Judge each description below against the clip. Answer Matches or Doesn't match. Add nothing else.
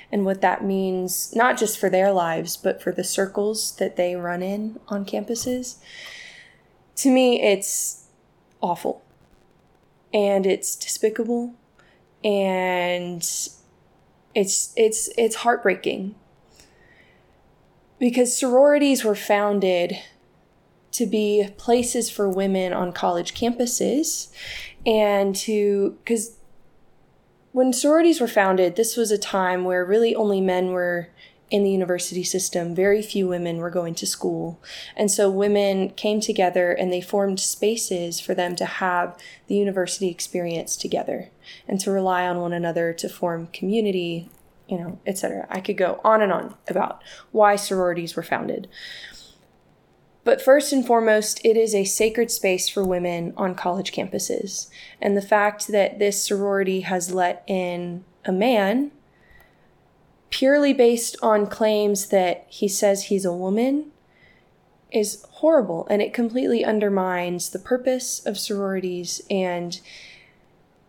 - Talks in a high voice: Matches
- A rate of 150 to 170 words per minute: Doesn't match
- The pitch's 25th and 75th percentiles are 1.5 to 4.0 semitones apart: Matches